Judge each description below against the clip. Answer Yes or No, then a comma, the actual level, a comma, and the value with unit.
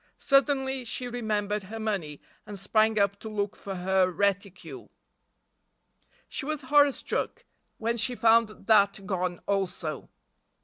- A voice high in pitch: Yes, high, 210 Hz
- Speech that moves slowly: Yes, slow, 130 wpm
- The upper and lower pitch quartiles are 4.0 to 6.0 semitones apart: No, average, 3.2 semitones